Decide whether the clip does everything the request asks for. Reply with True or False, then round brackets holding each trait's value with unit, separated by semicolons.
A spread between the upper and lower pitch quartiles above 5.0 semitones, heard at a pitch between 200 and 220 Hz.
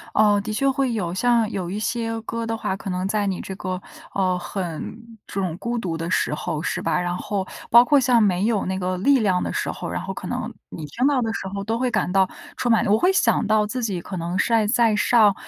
False (3.8 semitones; 210 Hz)